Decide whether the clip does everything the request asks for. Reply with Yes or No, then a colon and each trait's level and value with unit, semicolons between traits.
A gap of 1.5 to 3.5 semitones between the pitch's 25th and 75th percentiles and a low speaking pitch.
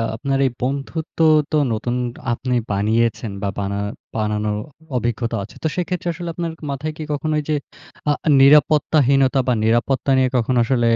No: average, 4.6 semitones; low, 130 Hz